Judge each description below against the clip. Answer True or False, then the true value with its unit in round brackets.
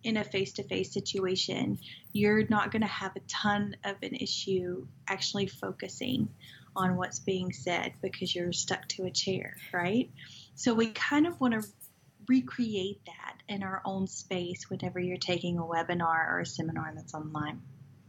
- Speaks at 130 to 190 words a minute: True (170 wpm)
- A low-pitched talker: False (190 Hz)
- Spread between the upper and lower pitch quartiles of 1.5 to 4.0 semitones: True (3.2 semitones)